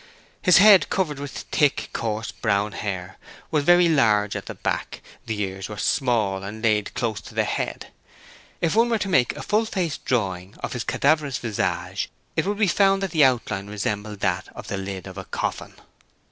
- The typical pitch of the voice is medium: No, low, 115 Hz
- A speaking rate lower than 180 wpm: No, average, 190 wpm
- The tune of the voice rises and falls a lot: Yes, wide, 8.3 semitones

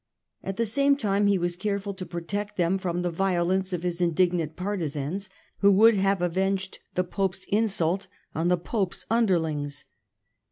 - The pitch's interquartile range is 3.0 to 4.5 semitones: No, narrow, 2.5 semitones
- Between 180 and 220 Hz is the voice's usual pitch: Yes, high, 190 Hz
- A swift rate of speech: No, average, 160 wpm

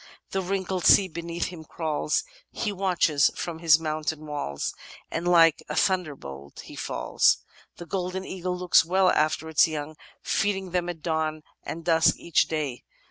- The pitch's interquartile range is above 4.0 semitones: No, average, 2.8 semitones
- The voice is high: No, medium, 165 Hz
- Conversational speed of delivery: Yes, average, 160 wpm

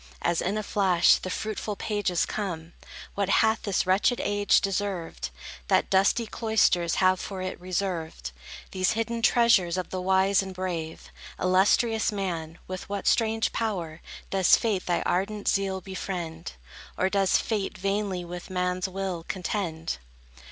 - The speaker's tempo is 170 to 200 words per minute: No, average, 145 wpm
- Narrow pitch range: Yes, narrow, 2.3 semitones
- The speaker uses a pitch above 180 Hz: Yes, high, 190 Hz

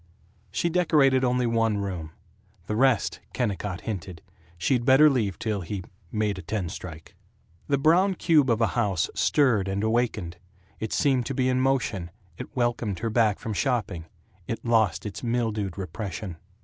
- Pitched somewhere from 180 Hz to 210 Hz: No, low, 110 Hz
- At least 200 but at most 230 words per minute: No, average, 160 wpm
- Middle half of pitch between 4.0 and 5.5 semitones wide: Yes, average, 4.5 semitones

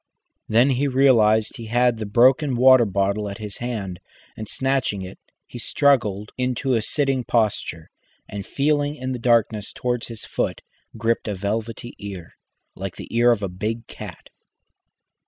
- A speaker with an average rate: Yes, average, 155 wpm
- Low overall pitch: Yes, low, 115 Hz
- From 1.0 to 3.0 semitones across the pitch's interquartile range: No, average, 3.6 semitones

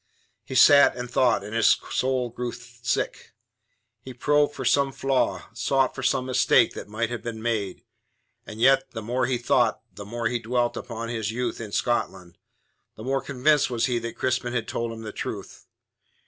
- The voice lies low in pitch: Yes, low, 120 Hz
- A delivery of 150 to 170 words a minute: No, average, 185 wpm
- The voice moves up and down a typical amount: No, narrow, 2.0 semitones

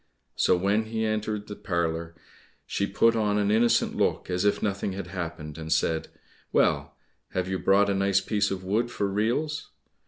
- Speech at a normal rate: Yes, average, 180 wpm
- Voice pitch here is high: No, low, 100 Hz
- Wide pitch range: No, average, 3.4 semitones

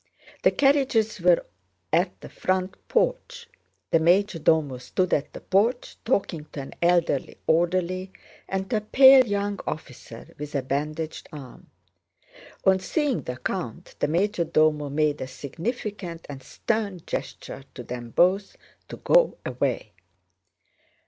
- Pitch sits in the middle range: Yes, medium, 175 Hz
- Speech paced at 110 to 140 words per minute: Yes, slow, 135 wpm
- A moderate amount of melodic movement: No, wide, 5.7 semitones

